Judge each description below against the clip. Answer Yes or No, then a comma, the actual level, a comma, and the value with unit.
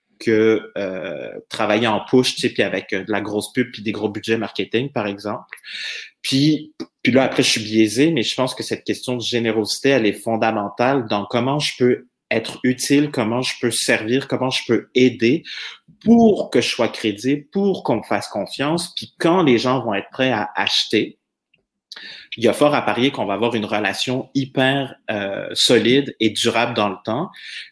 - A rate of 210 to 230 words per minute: No, average, 195 wpm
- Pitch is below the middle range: Yes, low, 120 Hz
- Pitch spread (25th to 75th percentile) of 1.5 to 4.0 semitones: Yes, average, 3.7 semitones